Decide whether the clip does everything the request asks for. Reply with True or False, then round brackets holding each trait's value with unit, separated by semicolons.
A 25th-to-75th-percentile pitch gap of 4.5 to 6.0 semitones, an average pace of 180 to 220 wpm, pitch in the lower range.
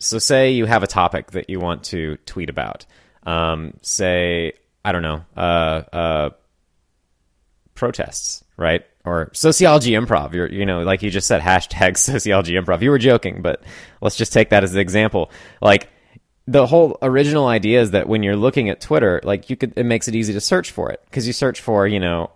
True (5.2 semitones; 200 wpm; 100 Hz)